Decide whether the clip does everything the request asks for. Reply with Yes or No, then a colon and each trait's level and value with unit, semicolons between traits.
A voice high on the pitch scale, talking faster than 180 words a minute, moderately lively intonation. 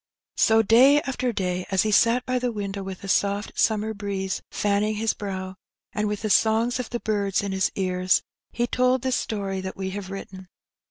Yes: high, 205 Hz; average, 200 wpm; average, 3.1 semitones